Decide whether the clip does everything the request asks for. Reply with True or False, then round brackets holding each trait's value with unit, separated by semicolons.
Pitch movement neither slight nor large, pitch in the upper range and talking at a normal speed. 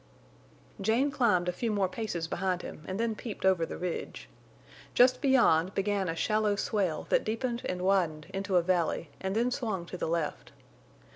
True (4.0 semitones; 195 Hz; 180 wpm)